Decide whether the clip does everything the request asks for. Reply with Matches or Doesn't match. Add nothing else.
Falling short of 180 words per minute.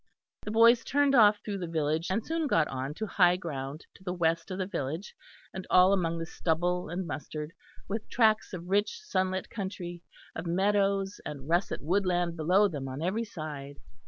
Doesn't match